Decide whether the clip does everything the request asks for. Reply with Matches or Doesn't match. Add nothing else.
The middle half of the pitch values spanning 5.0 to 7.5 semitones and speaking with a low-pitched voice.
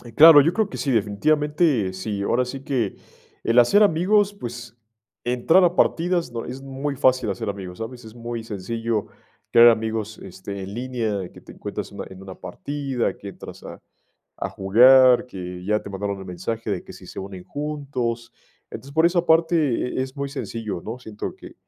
Matches